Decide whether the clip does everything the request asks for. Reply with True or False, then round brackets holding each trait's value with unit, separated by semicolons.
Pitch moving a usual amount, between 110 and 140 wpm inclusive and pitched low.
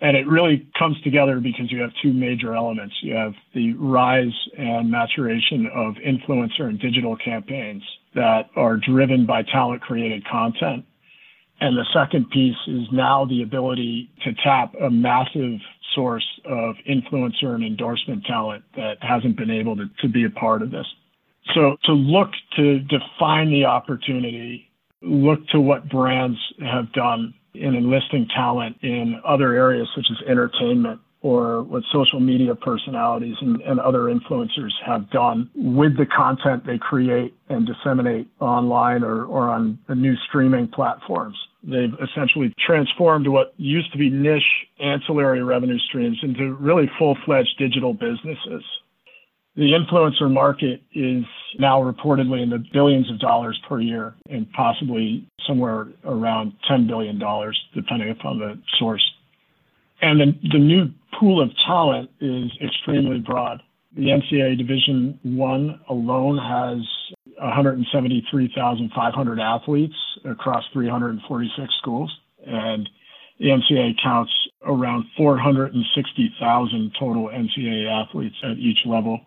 True (3.3 semitones; 135 wpm; 130 Hz)